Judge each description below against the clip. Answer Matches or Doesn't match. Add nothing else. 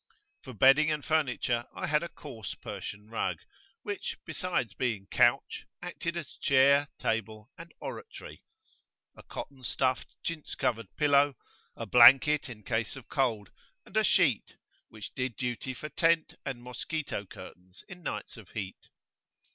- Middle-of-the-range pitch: Doesn't match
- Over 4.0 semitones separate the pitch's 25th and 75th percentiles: Matches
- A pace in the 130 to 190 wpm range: Matches